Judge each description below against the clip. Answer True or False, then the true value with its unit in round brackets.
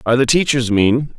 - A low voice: True (125 Hz)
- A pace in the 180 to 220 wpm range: True (200 wpm)